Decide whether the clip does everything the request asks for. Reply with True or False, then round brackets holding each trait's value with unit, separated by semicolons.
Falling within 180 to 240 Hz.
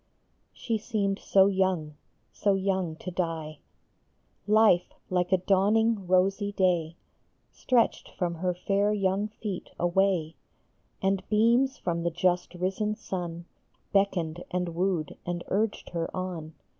True (185 Hz)